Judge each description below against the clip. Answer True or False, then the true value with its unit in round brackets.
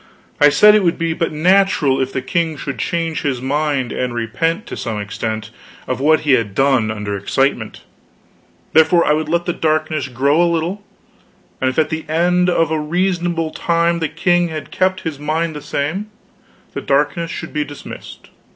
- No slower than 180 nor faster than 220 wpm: True (185 wpm)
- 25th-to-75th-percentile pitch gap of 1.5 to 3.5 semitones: False (4.0 semitones)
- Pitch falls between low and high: True (155 Hz)